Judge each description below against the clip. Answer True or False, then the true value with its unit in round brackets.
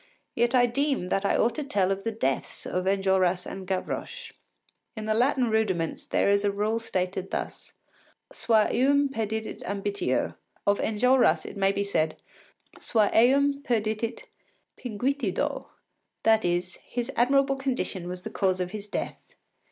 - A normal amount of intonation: True (4.3 semitones)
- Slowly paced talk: False (150 wpm)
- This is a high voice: True (215 Hz)